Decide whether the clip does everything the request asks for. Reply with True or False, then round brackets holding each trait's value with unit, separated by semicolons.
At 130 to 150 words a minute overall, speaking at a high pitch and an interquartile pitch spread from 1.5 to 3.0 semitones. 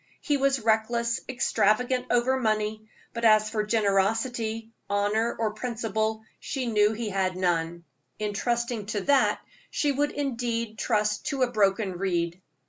True (140 wpm; 220 Hz; 2.5 semitones)